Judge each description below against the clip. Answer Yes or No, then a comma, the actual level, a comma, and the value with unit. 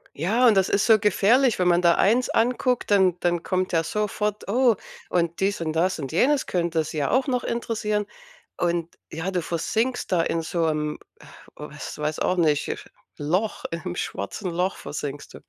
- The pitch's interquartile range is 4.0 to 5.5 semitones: Yes, average, 4.4 semitones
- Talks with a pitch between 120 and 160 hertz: No, medium, 180 Hz